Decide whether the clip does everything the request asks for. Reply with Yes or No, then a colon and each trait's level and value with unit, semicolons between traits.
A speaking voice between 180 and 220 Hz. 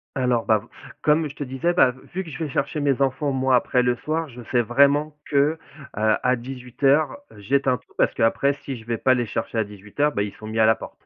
No: low, 130 Hz